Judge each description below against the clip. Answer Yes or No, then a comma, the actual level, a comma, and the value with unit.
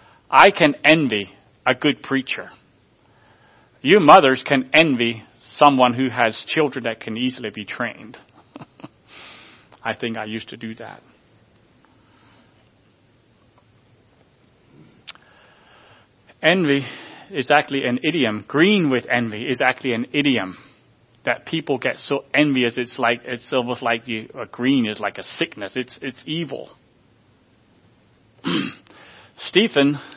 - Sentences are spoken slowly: Yes, slow, 115 wpm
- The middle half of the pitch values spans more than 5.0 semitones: No, average, 3.3 semitones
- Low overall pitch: Yes, low, 125 Hz